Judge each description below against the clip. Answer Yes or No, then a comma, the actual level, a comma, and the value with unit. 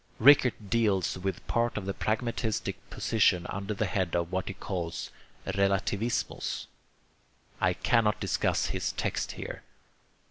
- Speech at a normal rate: No, slow, 130 wpm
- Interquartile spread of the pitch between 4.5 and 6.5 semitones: No, average, 3.0 semitones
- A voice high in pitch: No, low, 100 Hz